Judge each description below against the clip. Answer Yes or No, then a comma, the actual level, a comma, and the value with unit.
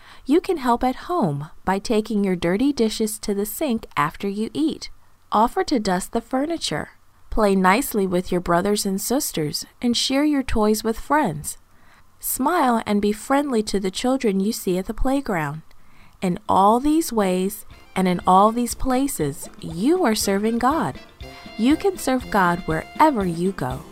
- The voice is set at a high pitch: Yes, high, 220 Hz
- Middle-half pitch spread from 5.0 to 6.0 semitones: Yes, wide, 5.6 semitones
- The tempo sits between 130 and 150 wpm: No, average, 165 wpm